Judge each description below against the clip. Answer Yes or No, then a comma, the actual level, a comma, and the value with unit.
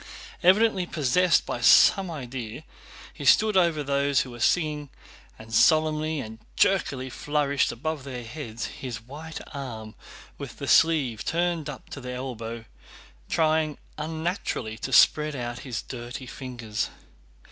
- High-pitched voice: No, medium, 140 Hz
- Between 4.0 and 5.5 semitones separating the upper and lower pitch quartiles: Yes, average, 4.6 semitones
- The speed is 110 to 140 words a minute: Yes, slow, 135 wpm